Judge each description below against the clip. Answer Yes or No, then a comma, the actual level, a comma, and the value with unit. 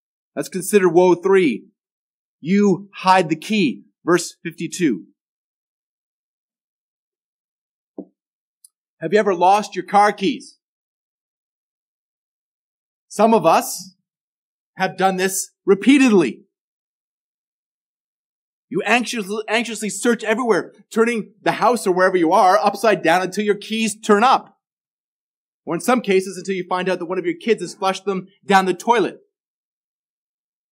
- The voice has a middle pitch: No, high, 195 Hz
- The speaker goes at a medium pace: No, slow, 120 wpm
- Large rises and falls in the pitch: No, average, 3.2 semitones